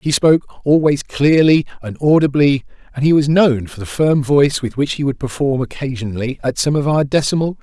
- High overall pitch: No, medium, 140 Hz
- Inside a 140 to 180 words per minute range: No, fast, 205 wpm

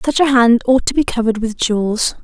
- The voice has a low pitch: No, high, 240 Hz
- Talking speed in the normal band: No, fast, 240 wpm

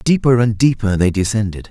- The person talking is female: No, male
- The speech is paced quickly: No, average, 175 wpm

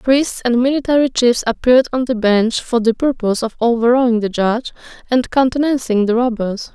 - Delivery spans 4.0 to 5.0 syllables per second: No, 5.5 syllables/s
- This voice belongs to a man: No, female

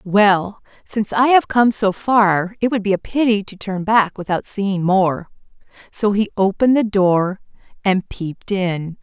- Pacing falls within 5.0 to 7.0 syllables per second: No, 4.2 syllables/s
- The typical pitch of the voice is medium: No, high, 200 Hz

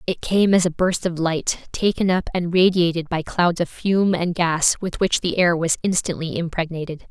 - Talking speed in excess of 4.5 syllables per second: Yes, 4.8 syllables/s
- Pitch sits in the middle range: Yes, medium, 175 Hz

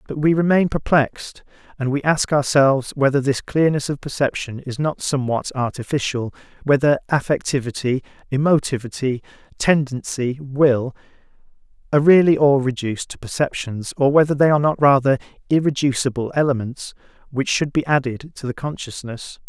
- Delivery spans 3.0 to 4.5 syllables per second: No, 5.5 syllables/s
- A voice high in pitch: No, low, 135 Hz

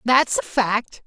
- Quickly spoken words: No, average, 170 wpm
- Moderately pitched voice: No, high, 235 Hz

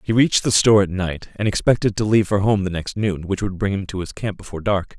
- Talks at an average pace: No, fast, 290 wpm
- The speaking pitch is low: Yes, low, 100 Hz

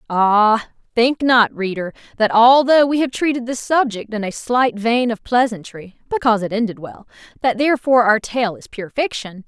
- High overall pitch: Yes, high, 230 Hz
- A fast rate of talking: No, average, 175 wpm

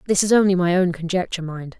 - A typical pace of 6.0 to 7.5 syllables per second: Yes, 6.9 syllables/s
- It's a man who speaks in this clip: No, female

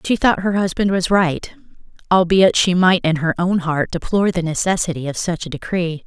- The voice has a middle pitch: Yes, medium, 175 Hz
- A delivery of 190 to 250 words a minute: Yes, average, 200 wpm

